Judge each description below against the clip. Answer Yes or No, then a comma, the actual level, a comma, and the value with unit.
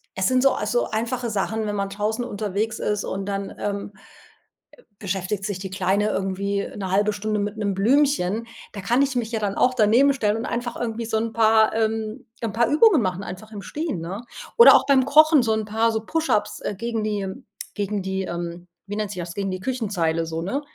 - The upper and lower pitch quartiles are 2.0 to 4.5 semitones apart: Yes, average, 2.9 semitones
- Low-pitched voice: No, high, 210 Hz